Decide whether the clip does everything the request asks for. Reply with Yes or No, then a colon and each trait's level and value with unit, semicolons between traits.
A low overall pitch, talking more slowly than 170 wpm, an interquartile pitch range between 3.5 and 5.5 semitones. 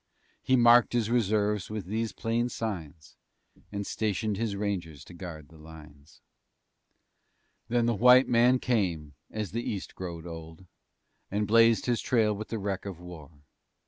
Yes: low, 105 Hz; average, 150 wpm; average, 5.1 semitones